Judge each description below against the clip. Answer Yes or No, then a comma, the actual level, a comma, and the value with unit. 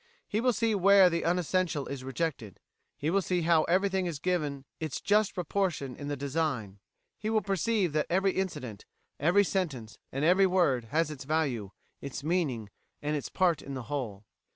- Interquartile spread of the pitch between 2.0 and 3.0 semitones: No, average, 5.3 semitones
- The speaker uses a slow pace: No, average, 175 wpm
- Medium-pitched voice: Yes, medium, 160 Hz